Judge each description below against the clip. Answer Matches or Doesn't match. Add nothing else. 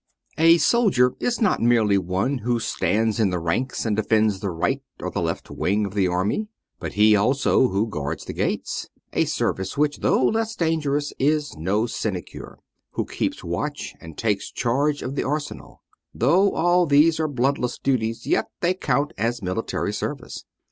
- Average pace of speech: Matches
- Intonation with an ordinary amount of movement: Doesn't match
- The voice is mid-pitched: Doesn't match